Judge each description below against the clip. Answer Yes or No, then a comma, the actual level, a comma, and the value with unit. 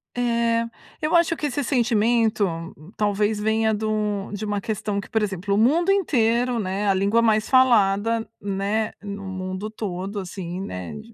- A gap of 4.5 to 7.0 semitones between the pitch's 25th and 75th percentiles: No, average, 2.7 semitones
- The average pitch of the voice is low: No, high, 215 Hz